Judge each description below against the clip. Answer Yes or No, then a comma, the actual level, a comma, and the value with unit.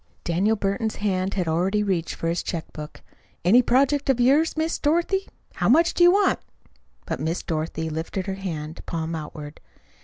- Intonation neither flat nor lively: No, wide, 8.0 semitones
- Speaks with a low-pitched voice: No, high, 195 Hz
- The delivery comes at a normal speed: Yes, average, 175 wpm